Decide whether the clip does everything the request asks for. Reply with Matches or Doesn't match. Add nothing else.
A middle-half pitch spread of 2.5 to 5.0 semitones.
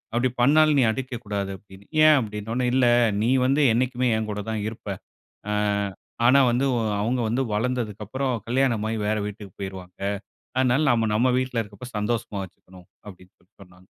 Matches